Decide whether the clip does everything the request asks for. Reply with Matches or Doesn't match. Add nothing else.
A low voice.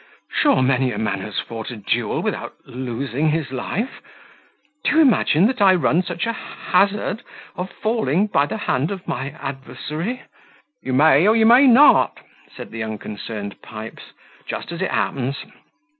Doesn't match